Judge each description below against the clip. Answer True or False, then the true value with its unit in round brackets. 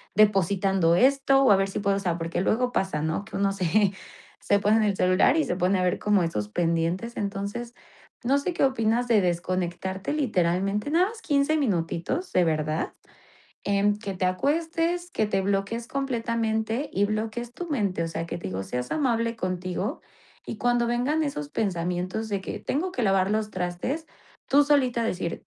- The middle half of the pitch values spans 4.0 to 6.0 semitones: True (5.0 semitones)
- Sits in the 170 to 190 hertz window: False (205 Hz)